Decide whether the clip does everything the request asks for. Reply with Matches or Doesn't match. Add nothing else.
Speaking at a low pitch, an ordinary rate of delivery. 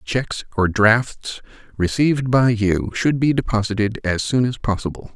Matches